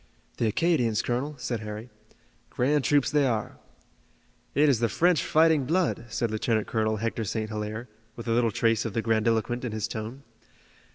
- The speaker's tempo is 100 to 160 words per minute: No, average, 170 wpm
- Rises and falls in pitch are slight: No, average, 3.9 semitones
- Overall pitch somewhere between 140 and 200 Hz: No, low, 115 Hz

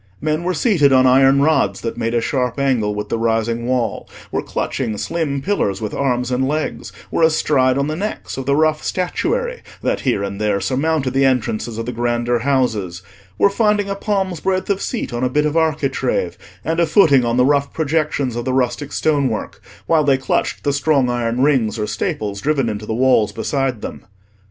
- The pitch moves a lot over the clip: No, average, 4.7 semitones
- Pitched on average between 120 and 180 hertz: Yes, low, 135 Hz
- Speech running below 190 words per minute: No, average, 200 wpm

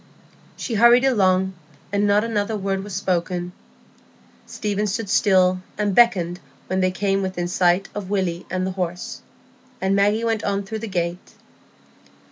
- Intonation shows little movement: Yes, narrow, 2.1 semitones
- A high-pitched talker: Yes, high, 195 Hz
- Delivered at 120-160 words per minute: Yes, average, 150 wpm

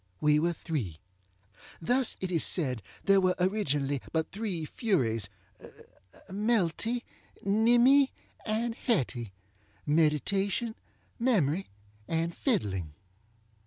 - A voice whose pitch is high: No, medium, 170 Hz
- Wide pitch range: Yes, wide, 8.0 semitones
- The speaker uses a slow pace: Yes, slow, 85 wpm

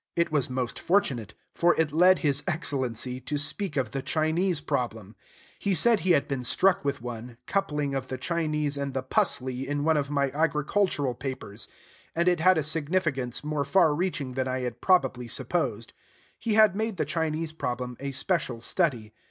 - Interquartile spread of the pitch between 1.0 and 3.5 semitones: No, average, 4.7 semitones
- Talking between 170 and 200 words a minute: Yes, average, 180 wpm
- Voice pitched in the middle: Yes, medium, 145 Hz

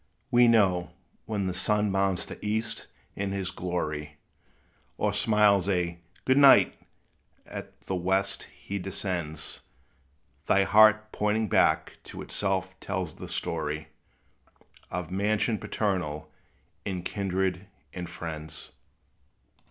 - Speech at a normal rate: No, slow, 115 wpm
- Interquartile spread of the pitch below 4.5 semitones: Yes, average, 2.9 semitones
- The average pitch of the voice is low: Yes, very low, 95 Hz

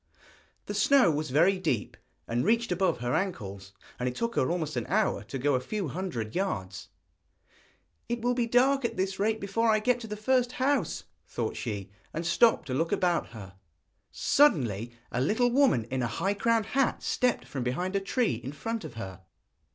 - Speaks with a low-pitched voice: No, medium, 185 Hz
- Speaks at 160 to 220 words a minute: Yes, average, 190 wpm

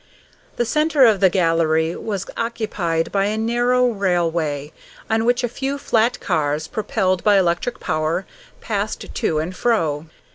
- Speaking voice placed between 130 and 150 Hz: No, high, 195 Hz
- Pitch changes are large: Yes, wide, 6.1 semitones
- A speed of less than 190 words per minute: Yes, average, 145 wpm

